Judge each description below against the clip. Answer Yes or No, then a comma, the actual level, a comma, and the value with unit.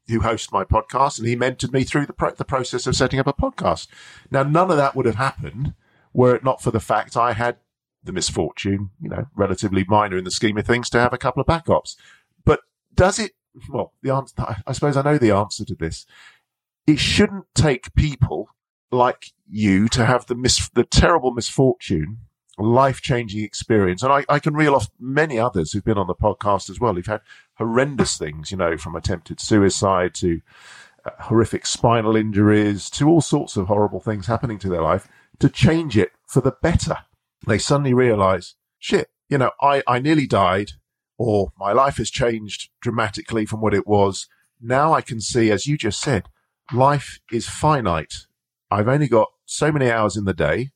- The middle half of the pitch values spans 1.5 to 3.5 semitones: No, average, 4.7 semitones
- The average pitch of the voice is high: No, low, 115 Hz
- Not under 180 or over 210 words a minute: Yes, average, 195 wpm